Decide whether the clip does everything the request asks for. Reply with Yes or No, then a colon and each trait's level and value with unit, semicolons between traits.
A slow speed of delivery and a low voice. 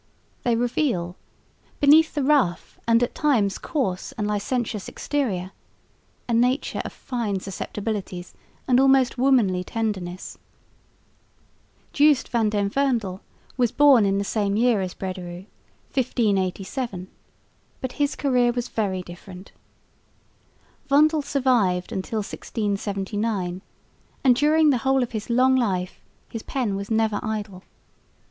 No: slow, 120 wpm; high, 225 Hz